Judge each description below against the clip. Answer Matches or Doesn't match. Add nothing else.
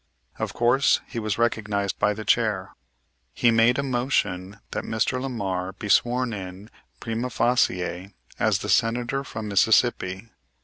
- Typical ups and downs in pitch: Matches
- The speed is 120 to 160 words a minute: Matches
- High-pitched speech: Doesn't match